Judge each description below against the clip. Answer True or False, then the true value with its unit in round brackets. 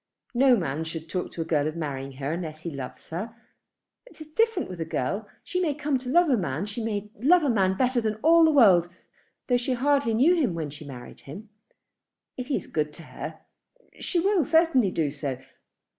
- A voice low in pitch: False (210 Hz)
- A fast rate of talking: True (215 wpm)